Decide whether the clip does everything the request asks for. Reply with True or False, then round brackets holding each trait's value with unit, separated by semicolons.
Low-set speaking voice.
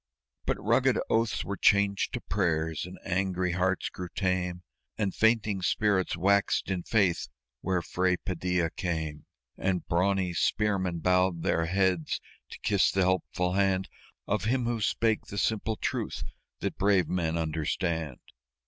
True (95 Hz)